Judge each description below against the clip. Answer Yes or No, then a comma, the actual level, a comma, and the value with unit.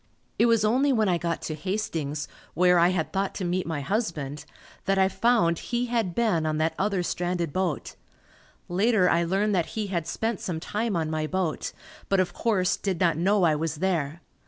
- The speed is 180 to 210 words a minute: Yes, average, 200 wpm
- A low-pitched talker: No, medium, 180 Hz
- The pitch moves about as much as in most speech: Yes, average, 4.2 semitones